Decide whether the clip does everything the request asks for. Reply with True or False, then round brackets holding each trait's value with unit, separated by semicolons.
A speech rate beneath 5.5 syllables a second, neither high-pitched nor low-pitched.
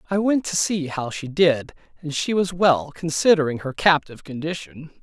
True (5.0 syllables/s; 160 Hz)